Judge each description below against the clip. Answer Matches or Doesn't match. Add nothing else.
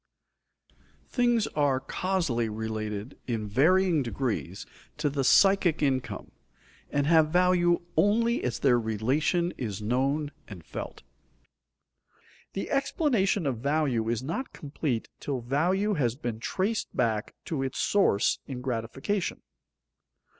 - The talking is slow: Matches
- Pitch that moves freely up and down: Matches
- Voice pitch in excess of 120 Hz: Matches